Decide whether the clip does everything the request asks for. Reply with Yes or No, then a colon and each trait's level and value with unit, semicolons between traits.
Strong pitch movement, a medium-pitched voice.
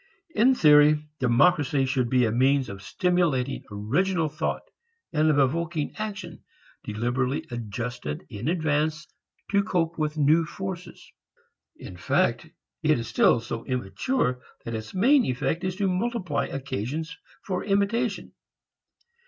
Yes: wide, 6.3 semitones; medium, 150 Hz